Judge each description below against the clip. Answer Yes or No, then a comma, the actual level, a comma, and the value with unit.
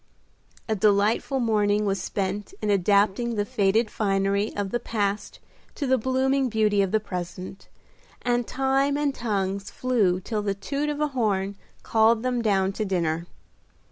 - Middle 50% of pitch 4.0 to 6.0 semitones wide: No, average, 3.5 semitones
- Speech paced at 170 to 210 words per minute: No, average, 155 wpm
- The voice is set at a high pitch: Yes, high, 210 Hz